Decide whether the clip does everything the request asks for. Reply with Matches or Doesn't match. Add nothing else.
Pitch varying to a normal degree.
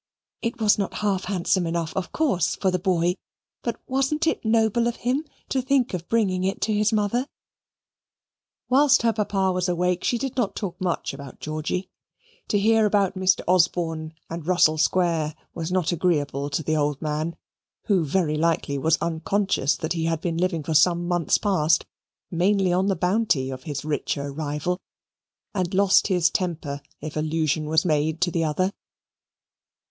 Matches